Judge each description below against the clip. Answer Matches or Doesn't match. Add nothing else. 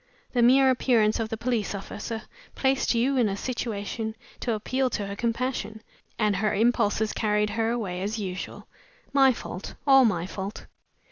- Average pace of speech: Matches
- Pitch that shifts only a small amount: Doesn't match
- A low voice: Doesn't match